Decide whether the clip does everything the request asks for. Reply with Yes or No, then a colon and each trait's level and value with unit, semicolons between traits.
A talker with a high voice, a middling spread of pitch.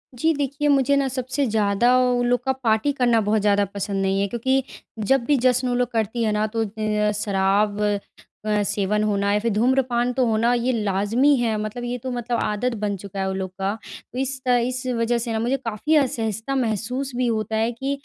Yes: high, 230 Hz; average, 3.2 semitones